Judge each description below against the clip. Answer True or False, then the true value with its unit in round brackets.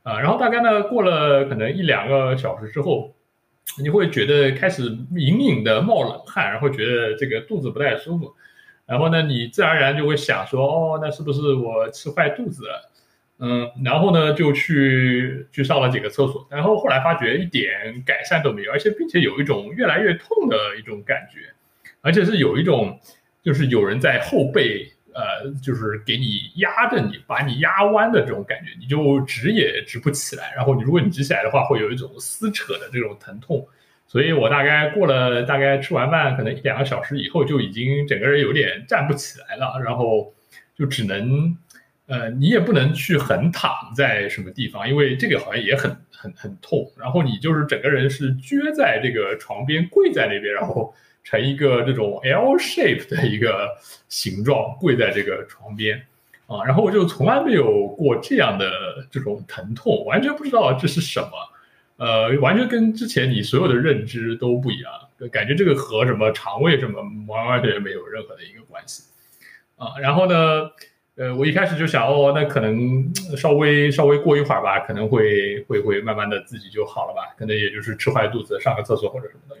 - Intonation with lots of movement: False (4.4 semitones)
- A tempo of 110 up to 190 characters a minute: False (295 characters per minute)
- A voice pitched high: False (140 Hz)